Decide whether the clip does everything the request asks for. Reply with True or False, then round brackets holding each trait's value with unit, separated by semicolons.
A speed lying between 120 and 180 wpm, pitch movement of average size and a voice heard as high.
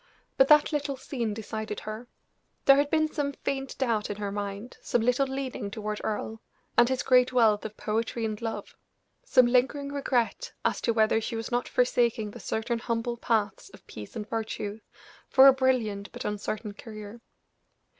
True (175 wpm; 3.4 semitones; 230 Hz)